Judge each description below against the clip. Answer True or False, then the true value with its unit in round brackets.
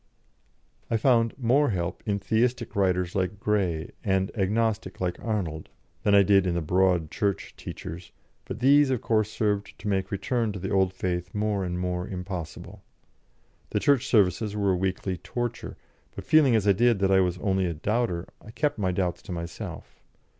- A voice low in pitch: True (100 Hz)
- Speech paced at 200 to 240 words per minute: False (180 wpm)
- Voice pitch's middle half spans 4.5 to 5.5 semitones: False (3.3 semitones)